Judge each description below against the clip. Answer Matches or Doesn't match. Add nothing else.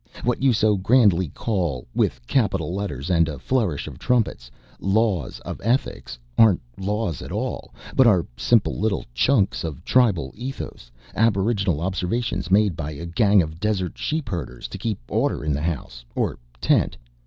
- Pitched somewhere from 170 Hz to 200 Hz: Doesn't match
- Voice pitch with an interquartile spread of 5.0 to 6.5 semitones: Matches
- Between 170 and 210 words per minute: Doesn't match